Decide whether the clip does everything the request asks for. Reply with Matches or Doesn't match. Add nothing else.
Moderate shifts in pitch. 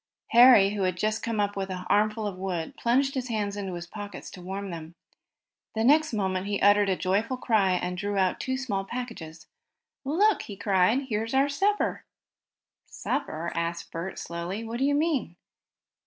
Matches